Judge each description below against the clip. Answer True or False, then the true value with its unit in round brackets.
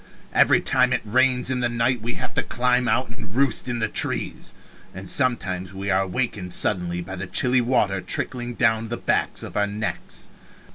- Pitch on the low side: True (115 Hz)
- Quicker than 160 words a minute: True (190 wpm)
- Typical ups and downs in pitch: True (4.4 semitones)